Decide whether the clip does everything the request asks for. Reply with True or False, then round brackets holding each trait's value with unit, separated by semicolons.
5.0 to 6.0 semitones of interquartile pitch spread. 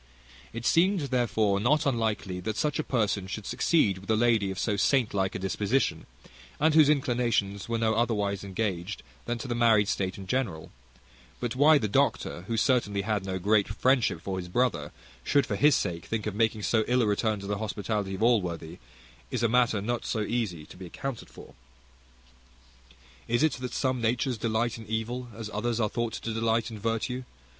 False (3.3 semitones)